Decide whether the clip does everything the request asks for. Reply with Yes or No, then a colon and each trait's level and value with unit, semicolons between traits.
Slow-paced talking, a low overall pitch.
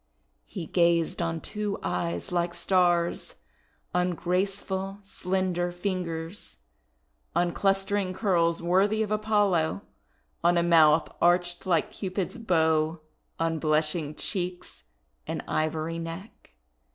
No: slow, 105 wpm; medium, 175 Hz